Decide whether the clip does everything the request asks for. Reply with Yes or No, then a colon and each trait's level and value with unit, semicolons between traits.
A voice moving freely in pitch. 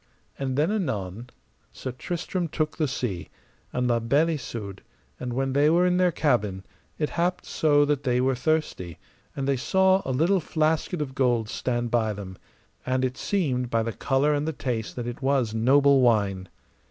No: average, 4.5 semitones